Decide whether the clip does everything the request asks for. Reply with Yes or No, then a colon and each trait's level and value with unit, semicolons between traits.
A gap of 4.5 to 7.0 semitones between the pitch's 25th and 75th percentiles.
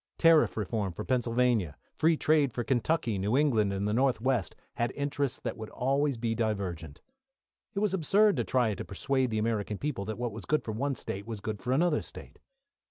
Yes: average, 4.8 semitones